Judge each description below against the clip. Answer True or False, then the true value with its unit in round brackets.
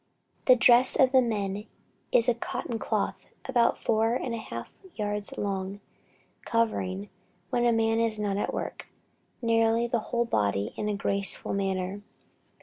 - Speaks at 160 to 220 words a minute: False (150 wpm)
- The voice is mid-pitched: False (220 Hz)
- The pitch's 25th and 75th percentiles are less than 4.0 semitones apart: True (2.9 semitones)